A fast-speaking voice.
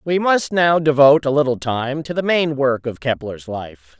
Yes: fast, 210 wpm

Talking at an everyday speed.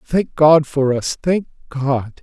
Yes: average, 160 wpm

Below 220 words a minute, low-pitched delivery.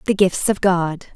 No: fast, 205 wpm; medium, 185 Hz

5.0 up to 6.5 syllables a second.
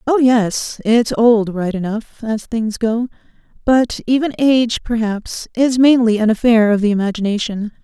No: 4.4 syllables/s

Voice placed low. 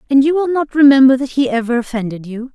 No: very high, 260 Hz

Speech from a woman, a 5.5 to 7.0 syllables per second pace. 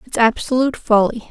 Yes: female; 6.3 syllables/s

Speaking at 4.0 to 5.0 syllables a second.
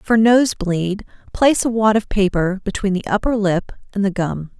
Yes: 4.8 syllables/s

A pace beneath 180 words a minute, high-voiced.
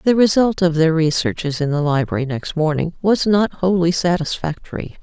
No: average, 165 wpm; medium, 170 Hz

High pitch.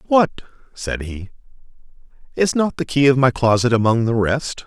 No: low, 130 Hz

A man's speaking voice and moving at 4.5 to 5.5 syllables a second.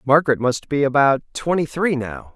Yes: male; 5.1 syllables/s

